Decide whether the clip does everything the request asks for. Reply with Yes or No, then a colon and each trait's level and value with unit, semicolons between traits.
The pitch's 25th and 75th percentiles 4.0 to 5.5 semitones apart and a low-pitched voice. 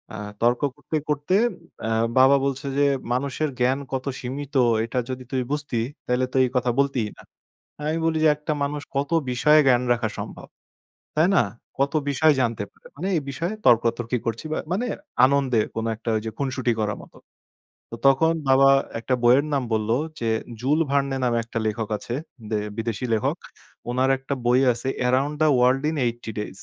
No: average, 3.2 semitones; low, 130 Hz